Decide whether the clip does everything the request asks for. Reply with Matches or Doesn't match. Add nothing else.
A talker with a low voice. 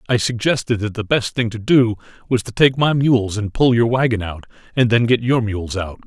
Matches